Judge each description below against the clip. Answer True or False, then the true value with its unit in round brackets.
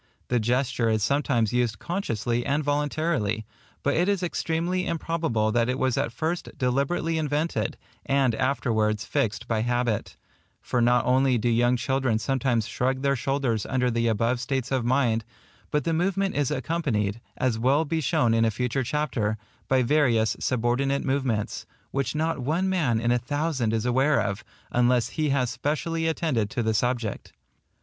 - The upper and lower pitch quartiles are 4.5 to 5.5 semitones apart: False (4.0 semitones)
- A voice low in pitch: True (130 Hz)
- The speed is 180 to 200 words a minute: False (165 wpm)